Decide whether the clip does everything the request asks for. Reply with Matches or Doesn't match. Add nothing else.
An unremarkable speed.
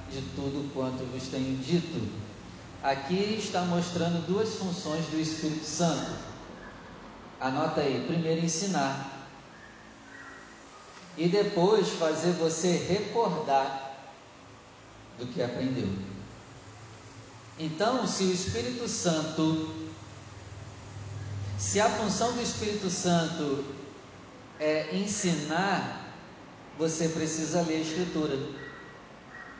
Doesn't match